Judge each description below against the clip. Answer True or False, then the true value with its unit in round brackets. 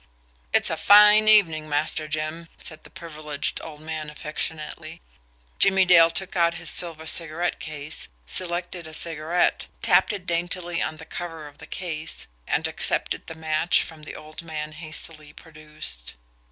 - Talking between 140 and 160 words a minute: True (150 wpm)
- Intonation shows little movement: True (2.1 semitones)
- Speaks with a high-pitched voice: False (160 Hz)